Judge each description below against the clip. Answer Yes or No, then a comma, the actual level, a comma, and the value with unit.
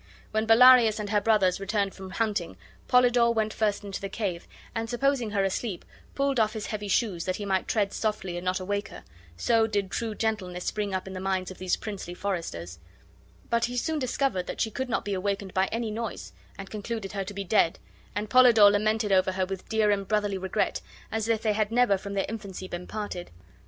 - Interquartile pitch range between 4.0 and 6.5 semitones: No, average, 2.8 semitones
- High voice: Yes, high, 205 Hz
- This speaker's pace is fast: Yes, fast, 215 wpm